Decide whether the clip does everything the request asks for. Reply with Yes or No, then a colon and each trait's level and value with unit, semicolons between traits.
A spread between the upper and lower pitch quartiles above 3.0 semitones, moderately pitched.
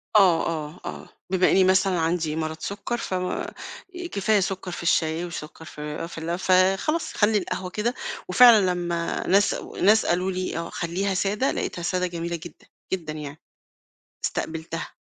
No: average, 2.7 semitones; medium, 180 Hz